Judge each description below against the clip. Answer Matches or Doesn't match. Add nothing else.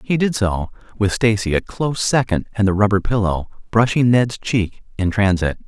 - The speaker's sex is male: Matches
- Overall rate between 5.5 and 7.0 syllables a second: Doesn't match